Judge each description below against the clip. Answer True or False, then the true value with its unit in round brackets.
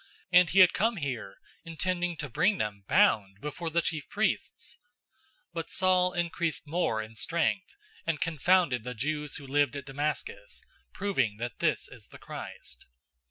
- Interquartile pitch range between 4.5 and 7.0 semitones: True (5.6 semitones)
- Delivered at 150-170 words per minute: True (160 wpm)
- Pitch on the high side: False (160 Hz)